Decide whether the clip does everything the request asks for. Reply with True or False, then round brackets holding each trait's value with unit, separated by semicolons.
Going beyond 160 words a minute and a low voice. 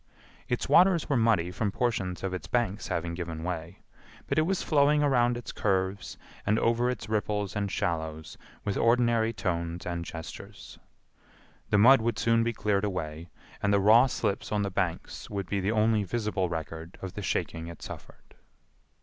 True (175 wpm; 100 Hz)